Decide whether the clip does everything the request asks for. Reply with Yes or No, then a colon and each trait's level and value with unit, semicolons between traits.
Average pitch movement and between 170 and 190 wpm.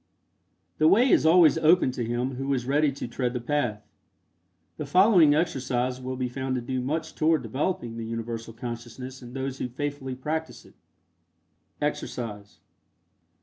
No: average, 3.8 semitones; average, 155 wpm